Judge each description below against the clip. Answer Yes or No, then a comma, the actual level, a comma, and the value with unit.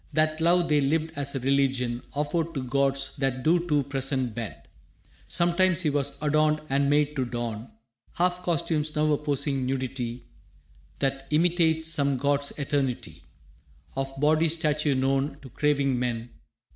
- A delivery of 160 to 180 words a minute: No, average, 145 wpm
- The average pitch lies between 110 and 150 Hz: Yes, medium, 140 Hz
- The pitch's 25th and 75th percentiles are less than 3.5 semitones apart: Yes, narrow, 2.5 semitones